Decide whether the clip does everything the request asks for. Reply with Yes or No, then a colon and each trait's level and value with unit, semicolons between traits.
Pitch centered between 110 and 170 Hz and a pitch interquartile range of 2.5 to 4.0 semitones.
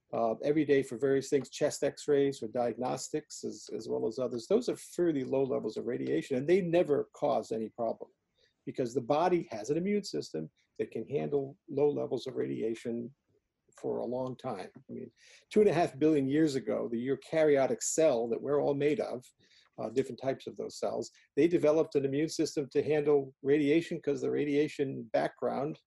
Yes: medium, 140 Hz; average, 2.8 semitones